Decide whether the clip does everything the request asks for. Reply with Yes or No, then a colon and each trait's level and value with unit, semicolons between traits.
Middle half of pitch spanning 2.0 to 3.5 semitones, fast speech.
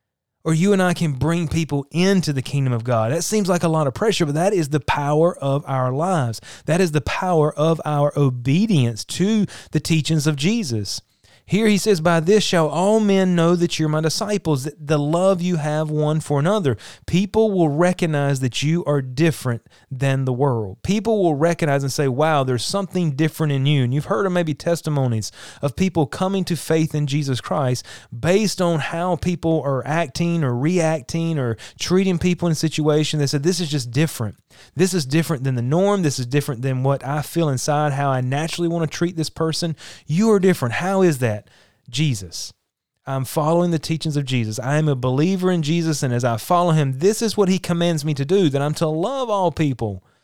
No: average, 4.0 semitones; fast, 210 wpm